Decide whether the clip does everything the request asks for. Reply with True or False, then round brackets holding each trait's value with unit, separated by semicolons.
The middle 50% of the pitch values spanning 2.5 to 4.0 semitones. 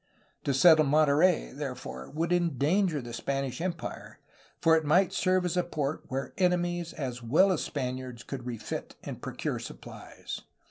False (5.1 semitones)